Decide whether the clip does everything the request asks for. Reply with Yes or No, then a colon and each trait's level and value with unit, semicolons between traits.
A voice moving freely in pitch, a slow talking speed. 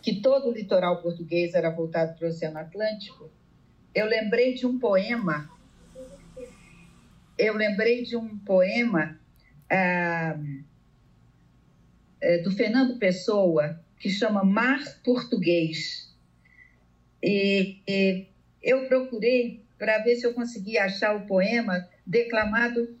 Yes: wide, 5.8 semitones; slow, 110 wpm